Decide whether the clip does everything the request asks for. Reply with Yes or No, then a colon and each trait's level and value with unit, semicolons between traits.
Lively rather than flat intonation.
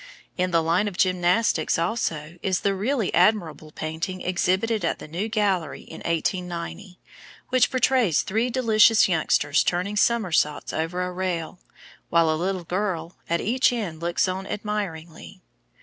No: average, 3.8 semitones